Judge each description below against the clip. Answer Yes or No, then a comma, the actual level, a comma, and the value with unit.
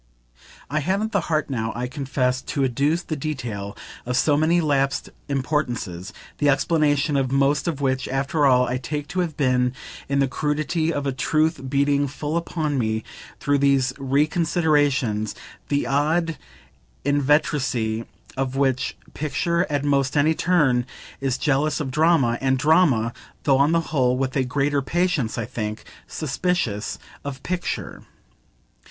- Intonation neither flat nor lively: Yes, average, 3.0 semitones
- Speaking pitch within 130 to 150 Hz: Yes, medium, 140 Hz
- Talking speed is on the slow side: No, average, 145 wpm